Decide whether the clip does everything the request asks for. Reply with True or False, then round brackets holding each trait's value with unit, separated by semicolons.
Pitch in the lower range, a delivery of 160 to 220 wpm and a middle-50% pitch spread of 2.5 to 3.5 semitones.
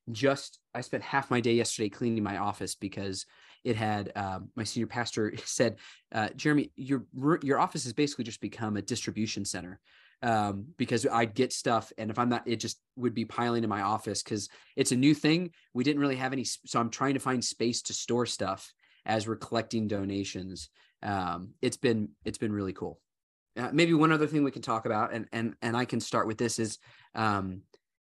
True (115 Hz; 205 wpm; 3.2 semitones)